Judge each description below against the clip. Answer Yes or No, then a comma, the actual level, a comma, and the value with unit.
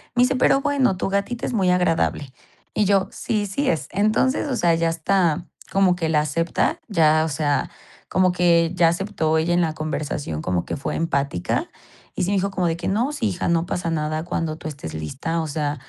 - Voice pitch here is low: No, medium, 170 Hz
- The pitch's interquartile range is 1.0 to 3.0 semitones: No, average, 4.0 semitones